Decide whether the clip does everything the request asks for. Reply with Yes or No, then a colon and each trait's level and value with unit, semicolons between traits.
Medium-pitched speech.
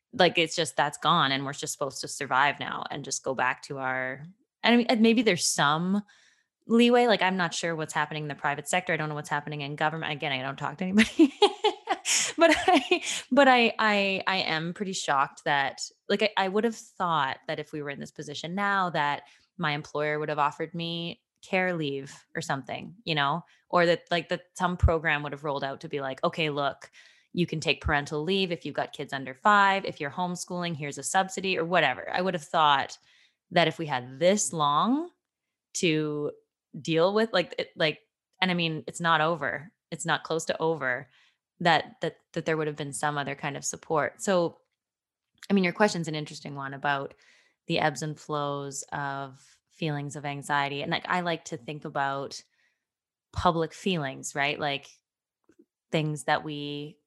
Yes: medium, 160 Hz